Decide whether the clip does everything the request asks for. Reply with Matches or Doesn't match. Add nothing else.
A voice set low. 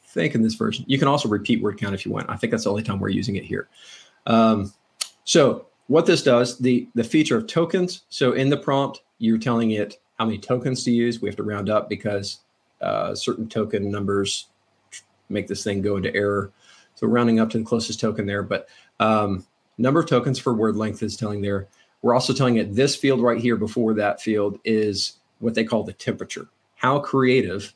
Matches